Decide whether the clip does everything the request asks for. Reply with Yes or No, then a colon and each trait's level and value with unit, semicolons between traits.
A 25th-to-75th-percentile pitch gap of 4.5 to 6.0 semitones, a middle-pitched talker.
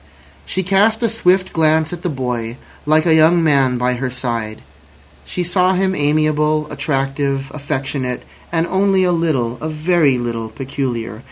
Yes: average, 5.3 semitones; medium, 150 Hz